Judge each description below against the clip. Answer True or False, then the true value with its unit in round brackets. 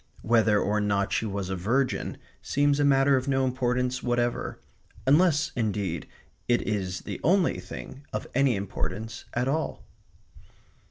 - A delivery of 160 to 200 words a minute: False (145 wpm)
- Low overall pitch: True (120 Hz)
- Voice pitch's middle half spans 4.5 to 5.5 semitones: True (4.8 semitones)